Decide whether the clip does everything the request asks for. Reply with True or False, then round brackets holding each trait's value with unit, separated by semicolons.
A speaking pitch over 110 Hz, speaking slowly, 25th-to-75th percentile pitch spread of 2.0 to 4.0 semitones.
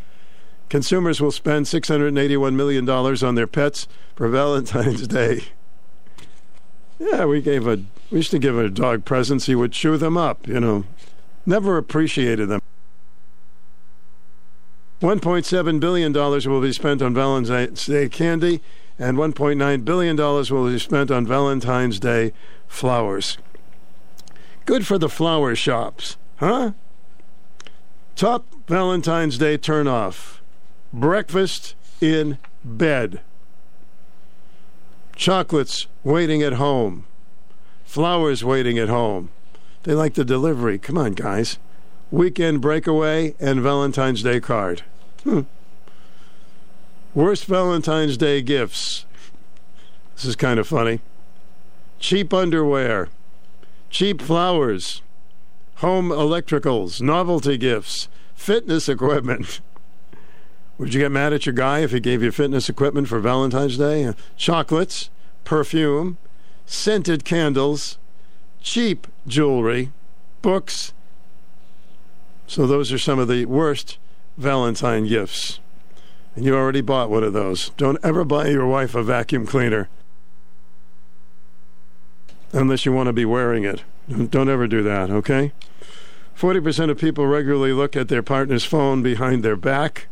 False (140 Hz; 125 wpm; 5.1 semitones)